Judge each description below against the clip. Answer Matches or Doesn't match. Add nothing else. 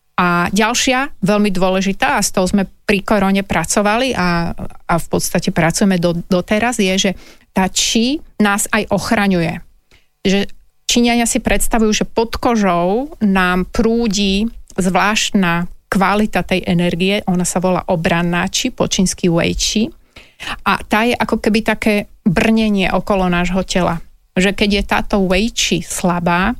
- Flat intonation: Doesn't match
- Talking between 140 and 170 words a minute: Matches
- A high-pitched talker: Matches